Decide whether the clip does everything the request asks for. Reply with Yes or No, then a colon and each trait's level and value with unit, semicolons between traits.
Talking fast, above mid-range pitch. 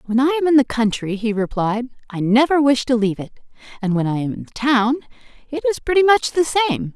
Yes: fast, 225 wpm; very high, 250 Hz